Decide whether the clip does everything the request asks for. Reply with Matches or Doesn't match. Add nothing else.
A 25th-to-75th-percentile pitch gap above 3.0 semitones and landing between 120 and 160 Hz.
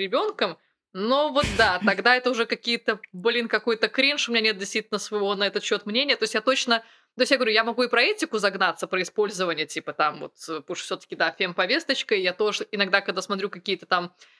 Doesn't match